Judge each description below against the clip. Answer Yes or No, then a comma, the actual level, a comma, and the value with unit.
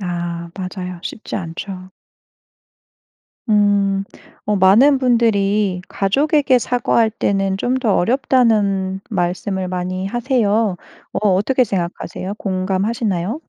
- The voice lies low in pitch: No, high, 200 Hz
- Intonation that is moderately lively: Yes, average, 3.6 semitones